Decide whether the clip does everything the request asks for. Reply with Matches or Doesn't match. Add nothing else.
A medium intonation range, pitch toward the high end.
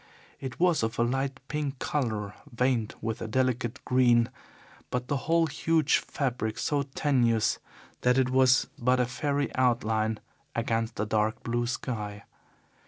Doesn't match